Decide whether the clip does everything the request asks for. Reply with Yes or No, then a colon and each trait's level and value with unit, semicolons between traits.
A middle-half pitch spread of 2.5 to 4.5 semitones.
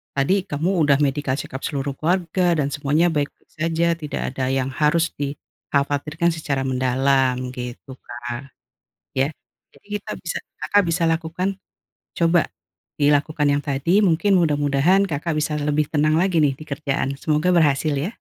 Yes: average, 3.0 semitones